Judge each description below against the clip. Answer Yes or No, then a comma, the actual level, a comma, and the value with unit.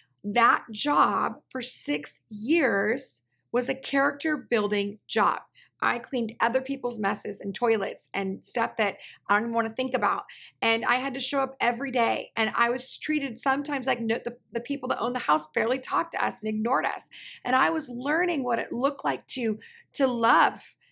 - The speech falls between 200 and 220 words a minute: No, average, 185 wpm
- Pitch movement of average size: Yes, average, 3.0 semitones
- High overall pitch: Yes, high, 240 Hz